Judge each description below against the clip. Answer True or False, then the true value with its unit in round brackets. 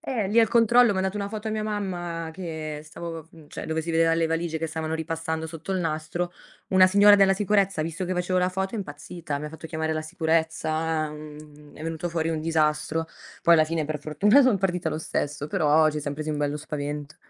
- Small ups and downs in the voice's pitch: False (3.3 semitones)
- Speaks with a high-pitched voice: False (165 Hz)